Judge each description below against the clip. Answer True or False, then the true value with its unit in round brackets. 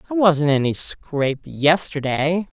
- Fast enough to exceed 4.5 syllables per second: False (4.4 syllables/s)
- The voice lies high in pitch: False (155 Hz)